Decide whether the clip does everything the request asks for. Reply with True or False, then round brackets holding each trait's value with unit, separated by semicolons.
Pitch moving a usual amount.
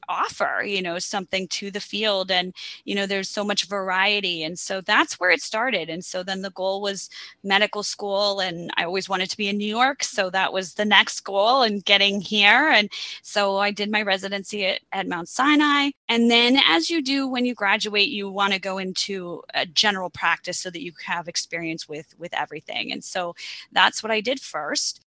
False (2.1 semitones)